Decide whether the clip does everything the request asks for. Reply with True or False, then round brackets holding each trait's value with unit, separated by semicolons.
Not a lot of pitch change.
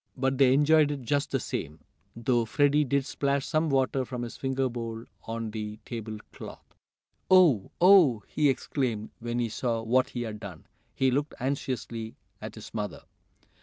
False (3.5 semitones)